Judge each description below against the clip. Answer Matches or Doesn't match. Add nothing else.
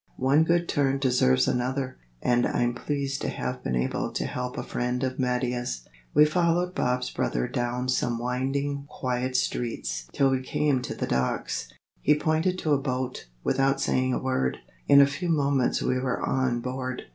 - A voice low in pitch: Matches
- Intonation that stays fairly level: Matches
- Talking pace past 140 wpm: Matches